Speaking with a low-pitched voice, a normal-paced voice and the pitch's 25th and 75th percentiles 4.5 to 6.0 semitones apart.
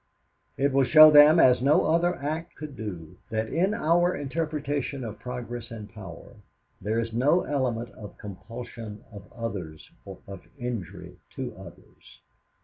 Yes: low, 125 Hz; average, 145 wpm; average, 5.3 semitones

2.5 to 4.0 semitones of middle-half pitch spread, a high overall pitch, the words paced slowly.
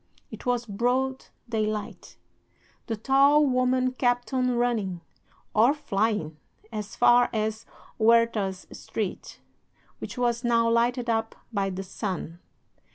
Yes: average, 2.8 semitones; high, 230 Hz; slow, 115 wpm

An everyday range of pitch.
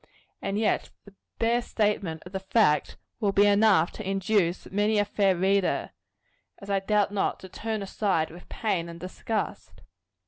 No: narrow, 2.2 semitones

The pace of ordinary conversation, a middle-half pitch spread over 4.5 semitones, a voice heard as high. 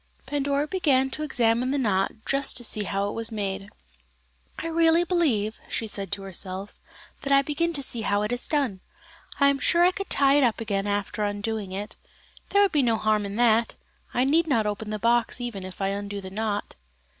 No: fast, 210 wpm; wide, 5.4 semitones; high, 225 Hz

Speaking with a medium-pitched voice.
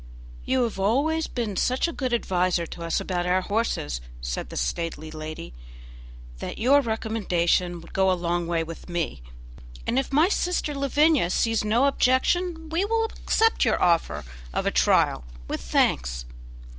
No: high, 210 Hz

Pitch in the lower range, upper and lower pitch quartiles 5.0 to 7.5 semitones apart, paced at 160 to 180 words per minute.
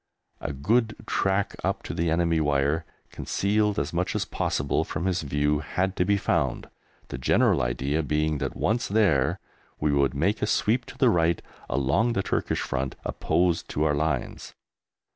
Yes: very low, 80 Hz; average, 5.3 semitones; average, 170 wpm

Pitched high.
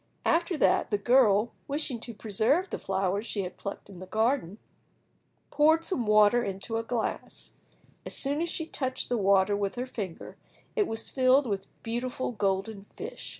Yes: high, 225 Hz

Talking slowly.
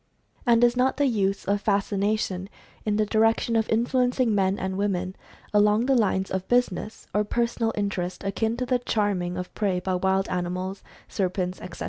No: average, 175 wpm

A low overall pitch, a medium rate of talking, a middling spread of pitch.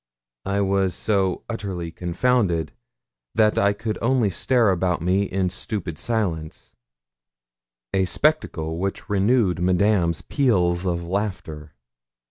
No: very low, 95 Hz; slow, 110 wpm; average, 3.6 semitones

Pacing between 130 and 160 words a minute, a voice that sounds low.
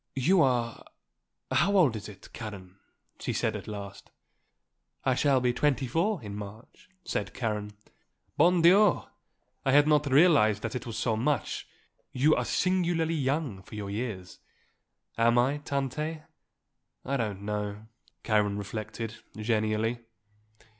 Yes: slow, 135 wpm; low, 120 Hz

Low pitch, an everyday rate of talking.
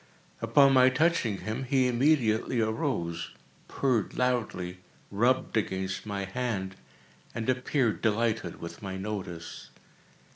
No: low, 110 Hz; slow, 110 wpm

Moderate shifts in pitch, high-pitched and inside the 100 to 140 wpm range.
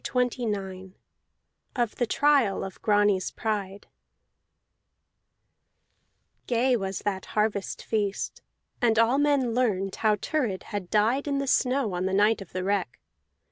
Yes: average, 4.2 semitones; high, 210 Hz; slow, 135 wpm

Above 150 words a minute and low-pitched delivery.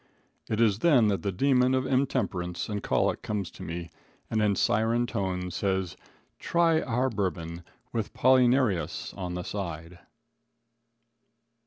No: average, 140 wpm; low, 105 Hz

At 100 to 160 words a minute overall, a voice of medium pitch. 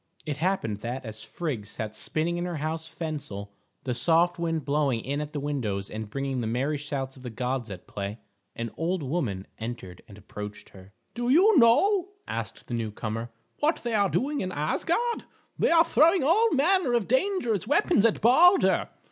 No: average, 180 wpm; medium, 150 Hz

